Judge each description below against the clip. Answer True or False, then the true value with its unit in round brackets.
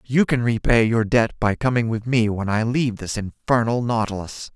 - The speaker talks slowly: False (200 wpm)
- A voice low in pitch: True (115 Hz)